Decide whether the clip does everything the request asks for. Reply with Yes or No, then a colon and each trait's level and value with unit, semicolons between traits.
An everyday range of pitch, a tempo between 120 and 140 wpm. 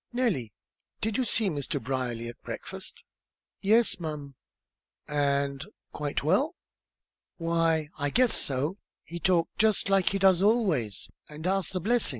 No: wide, 6.0 semitones; slow, 135 wpm